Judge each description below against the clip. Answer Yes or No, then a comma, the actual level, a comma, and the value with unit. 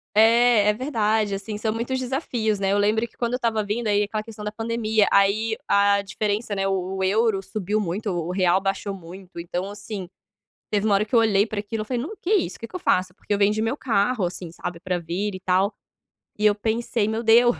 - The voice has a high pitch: Yes, high, 210 Hz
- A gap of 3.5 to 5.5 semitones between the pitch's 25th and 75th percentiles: No, narrow, 2.5 semitones